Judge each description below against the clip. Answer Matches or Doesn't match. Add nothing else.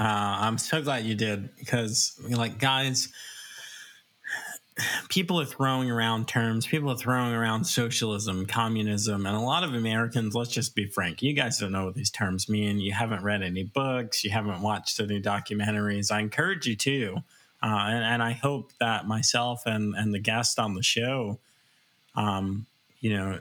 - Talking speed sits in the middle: Matches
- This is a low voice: Matches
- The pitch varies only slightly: Doesn't match